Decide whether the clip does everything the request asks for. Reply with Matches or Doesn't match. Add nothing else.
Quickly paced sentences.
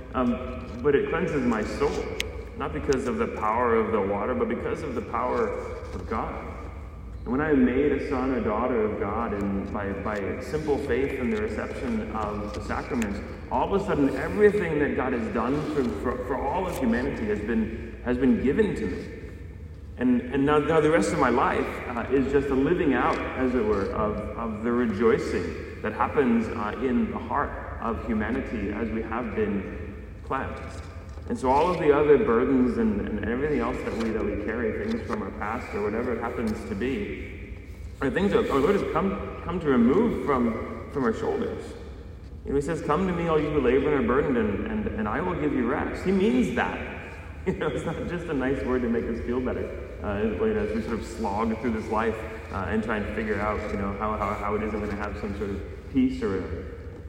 Matches